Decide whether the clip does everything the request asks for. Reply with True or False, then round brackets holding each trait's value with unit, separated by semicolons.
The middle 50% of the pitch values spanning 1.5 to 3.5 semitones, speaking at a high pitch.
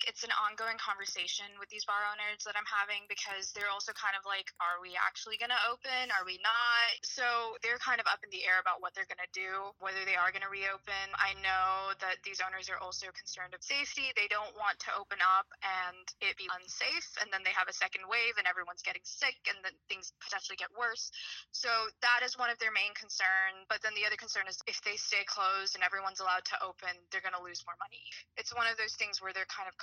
True (2.7 semitones; 200 Hz)